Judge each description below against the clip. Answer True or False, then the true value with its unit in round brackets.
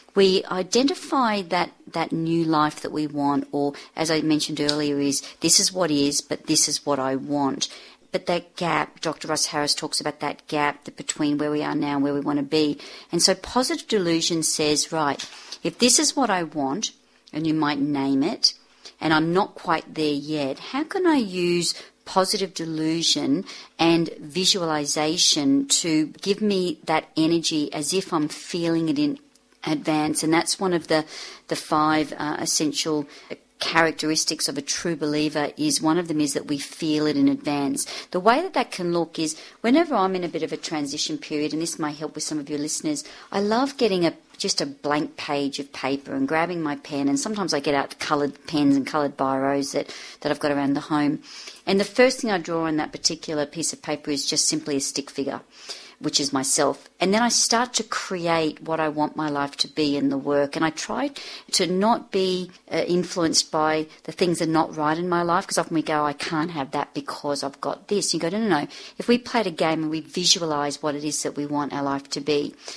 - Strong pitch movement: False (3.7 semitones)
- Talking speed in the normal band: False (215 wpm)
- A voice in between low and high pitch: True (155 Hz)